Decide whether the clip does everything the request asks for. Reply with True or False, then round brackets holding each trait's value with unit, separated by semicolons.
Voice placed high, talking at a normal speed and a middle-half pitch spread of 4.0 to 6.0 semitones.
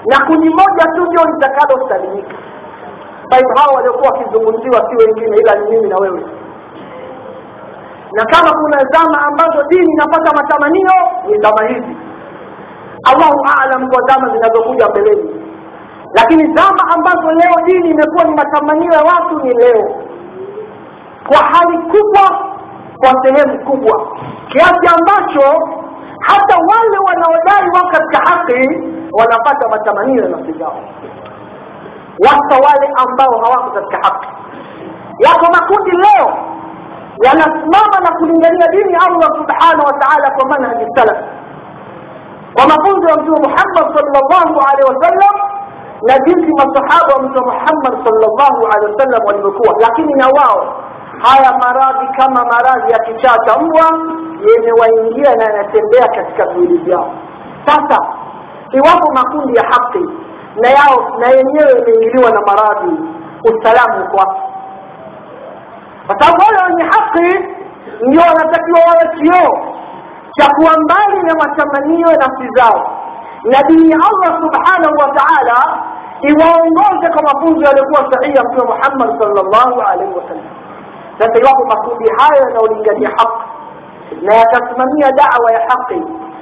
True (300 Hz; 110 wpm; 5.1 semitones)